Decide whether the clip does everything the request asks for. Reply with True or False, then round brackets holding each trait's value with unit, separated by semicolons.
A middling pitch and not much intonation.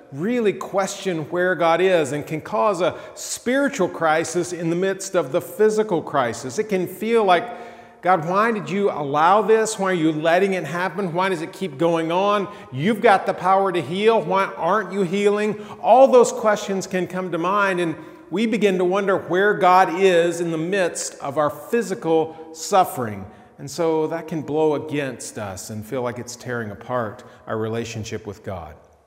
False (180 Hz; 4.3 semitones)